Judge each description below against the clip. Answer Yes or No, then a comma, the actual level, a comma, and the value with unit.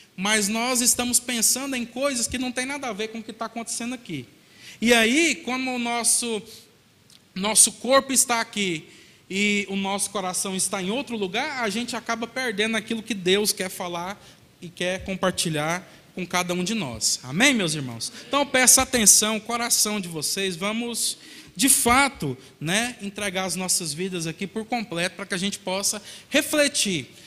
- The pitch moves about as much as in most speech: Yes, average, 4.4 semitones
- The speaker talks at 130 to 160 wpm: No, average, 175 wpm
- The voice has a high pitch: Yes, high, 210 Hz